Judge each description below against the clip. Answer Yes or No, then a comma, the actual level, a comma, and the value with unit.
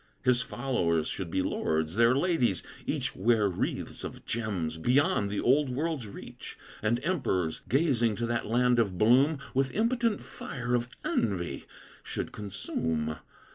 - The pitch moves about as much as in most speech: No, wide, 5.8 semitones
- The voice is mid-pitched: No, low, 120 Hz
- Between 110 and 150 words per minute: Yes, average, 140 wpm